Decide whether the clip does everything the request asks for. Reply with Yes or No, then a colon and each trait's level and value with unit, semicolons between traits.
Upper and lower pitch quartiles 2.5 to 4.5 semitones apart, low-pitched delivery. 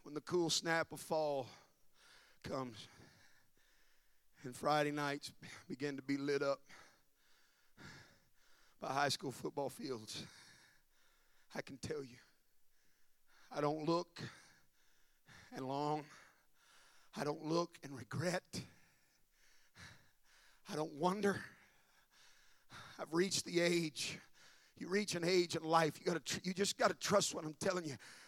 No: average, 3.3 semitones; medium, 155 Hz